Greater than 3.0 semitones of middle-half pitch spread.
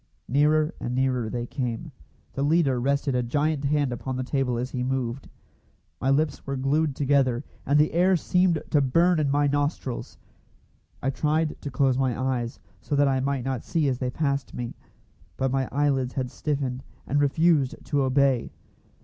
No: narrow, 2.4 semitones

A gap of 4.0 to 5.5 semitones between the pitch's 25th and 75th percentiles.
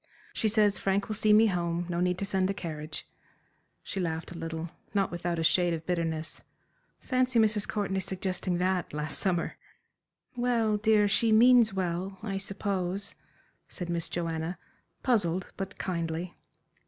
No: average, 3.3 semitones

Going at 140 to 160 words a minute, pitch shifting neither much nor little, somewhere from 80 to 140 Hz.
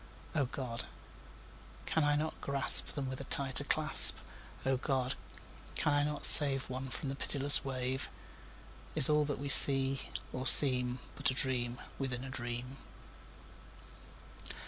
No: average, 145 wpm; narrow, 1.7 semitones; low, 135 Hz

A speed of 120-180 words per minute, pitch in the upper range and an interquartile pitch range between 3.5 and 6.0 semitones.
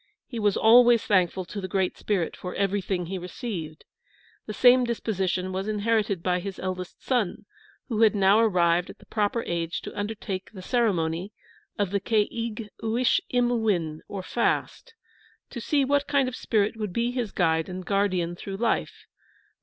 Yes: average, 175 wpm; high, 205 Hz; average, 3.9 semitones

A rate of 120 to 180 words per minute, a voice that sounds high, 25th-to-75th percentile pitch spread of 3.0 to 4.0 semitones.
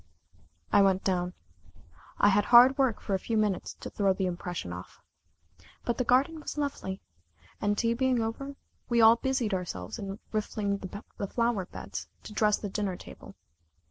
Yes: average, 165 wpm; high, 210 Hz; average, 3.7 semitones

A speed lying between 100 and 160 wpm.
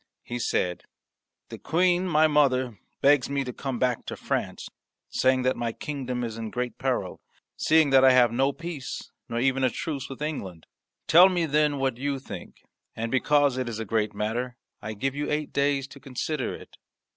No: average, 190 wpm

